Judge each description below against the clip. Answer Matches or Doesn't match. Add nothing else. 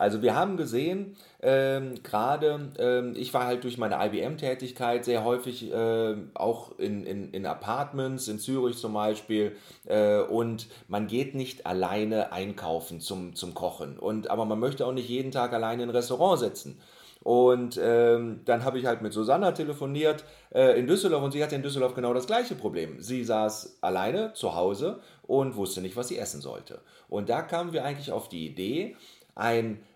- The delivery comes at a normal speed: Matches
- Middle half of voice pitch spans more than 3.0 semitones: Matches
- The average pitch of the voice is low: Matches